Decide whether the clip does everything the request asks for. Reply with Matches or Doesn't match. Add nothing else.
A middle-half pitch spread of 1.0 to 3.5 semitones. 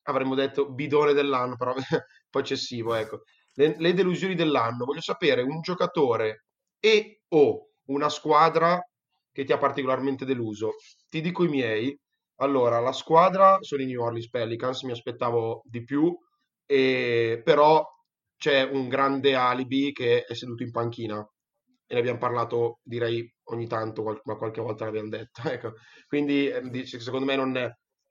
Doesn't match